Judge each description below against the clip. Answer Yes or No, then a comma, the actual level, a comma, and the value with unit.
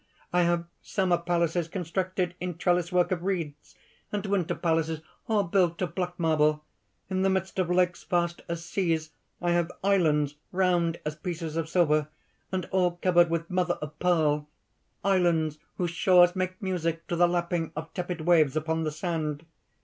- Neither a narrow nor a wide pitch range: No, narrow, 2.0 semitones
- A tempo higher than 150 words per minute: Yes, average, 165 wpm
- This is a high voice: No, medium, 175 Hz